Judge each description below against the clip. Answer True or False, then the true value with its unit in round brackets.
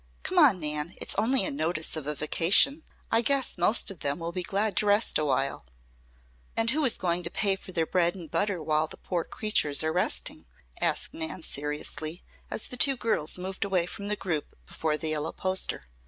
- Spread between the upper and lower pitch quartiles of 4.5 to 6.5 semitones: True (5.1 semitones)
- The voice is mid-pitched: True (180 Hz)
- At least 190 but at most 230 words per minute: True (200 wpm)